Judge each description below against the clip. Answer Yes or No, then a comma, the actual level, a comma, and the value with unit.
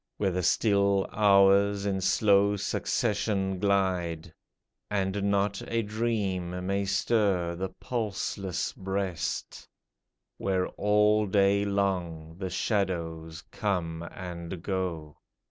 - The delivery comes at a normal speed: No, slow, 105 wpm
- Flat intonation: Yes, narrow, 2.0 semitones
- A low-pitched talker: Yes, very low, 95 Hz